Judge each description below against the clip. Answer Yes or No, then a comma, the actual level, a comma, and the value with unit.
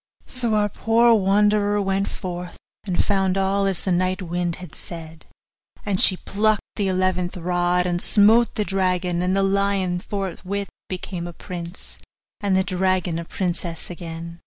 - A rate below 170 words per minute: Yes, average, 160 wpm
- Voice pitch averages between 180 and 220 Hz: Yes, medium, 185 Hz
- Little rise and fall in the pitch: Yes, narrow, 2.1 semitones